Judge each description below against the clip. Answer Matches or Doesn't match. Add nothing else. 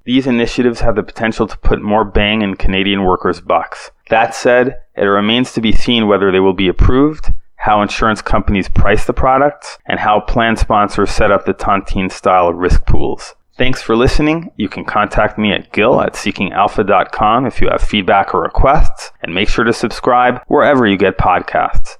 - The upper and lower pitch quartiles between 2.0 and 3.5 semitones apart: Doesn't match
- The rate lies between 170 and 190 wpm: Matches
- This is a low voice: Matches